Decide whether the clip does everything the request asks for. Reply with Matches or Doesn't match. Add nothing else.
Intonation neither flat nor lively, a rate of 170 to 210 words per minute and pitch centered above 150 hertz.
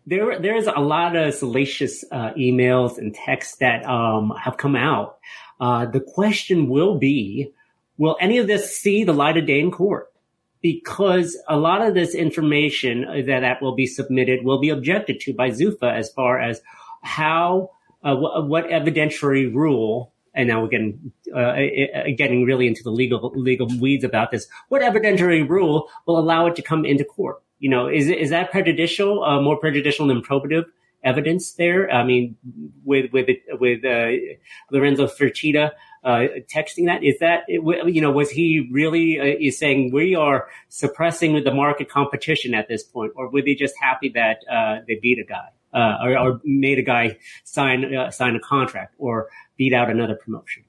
Doesn't match